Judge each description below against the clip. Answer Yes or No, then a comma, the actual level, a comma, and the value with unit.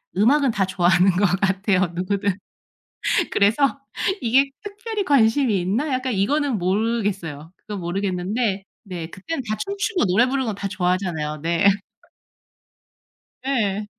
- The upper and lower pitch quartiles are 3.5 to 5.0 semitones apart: No, wide, 5.6 semitones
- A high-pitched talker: Yes, high, 205 Hz